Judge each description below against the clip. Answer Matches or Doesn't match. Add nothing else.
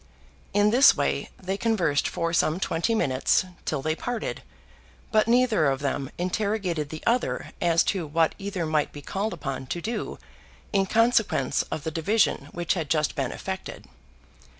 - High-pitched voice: Doesn't match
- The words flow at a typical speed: Matches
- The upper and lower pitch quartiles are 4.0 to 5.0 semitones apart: Doesn't match